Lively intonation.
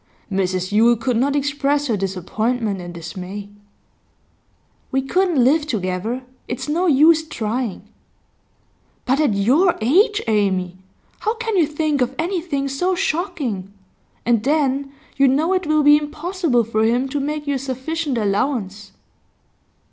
Yes: wide, 6.1 semitones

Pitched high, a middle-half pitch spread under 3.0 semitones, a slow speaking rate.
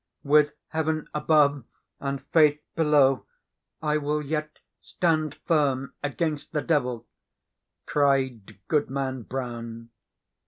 No: medium, 145 Hz; narrow, 2.4 semitones; slow, 95 wpm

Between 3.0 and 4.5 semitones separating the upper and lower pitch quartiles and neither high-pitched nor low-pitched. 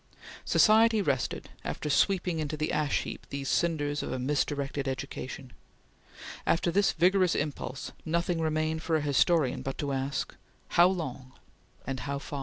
Yes: average, 3.7 semitones; medium, 150 Hz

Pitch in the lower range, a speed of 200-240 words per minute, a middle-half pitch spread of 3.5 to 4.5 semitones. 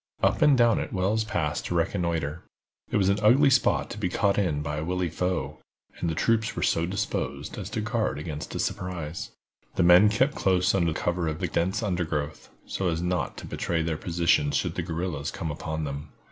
Yes: very low, 90 Hz; fast, 205 wpm; average, 3.9 semitones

